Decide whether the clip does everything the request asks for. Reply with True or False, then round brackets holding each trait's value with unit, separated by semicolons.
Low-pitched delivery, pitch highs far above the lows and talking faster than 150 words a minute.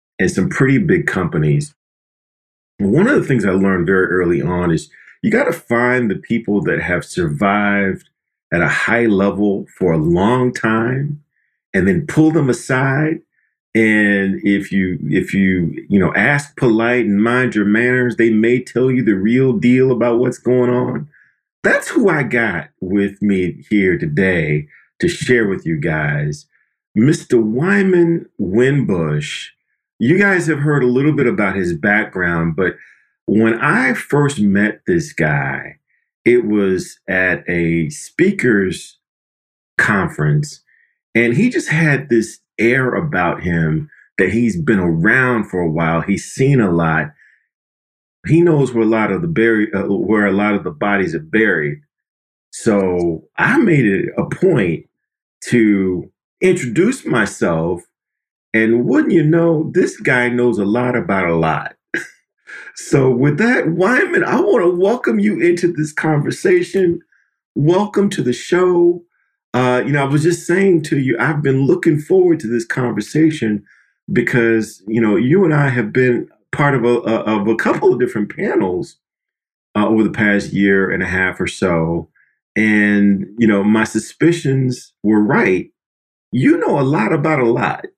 True (115 Hz; 6.7 semitones; 160 wpm)